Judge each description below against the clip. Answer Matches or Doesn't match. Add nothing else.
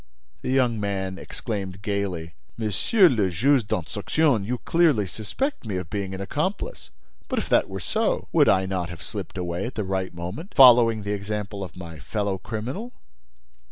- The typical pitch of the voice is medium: Doesn't match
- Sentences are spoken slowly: Doesn't match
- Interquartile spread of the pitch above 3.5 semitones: Matches